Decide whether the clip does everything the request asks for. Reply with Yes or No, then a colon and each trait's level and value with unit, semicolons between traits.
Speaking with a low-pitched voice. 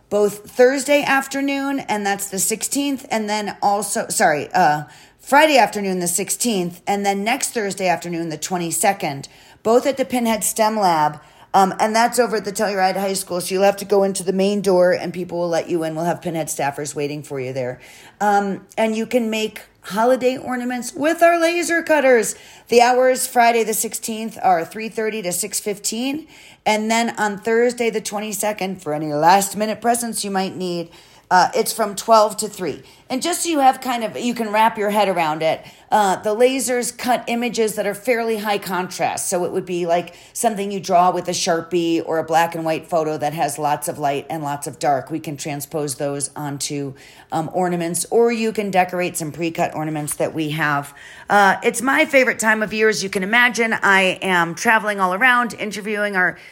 No: high, 200 Hz